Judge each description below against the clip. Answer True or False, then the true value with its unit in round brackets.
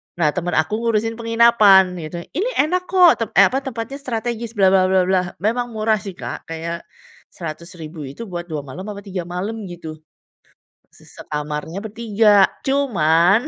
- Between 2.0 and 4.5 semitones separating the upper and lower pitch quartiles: False (4.9 semitones)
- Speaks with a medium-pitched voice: False (195 Hz)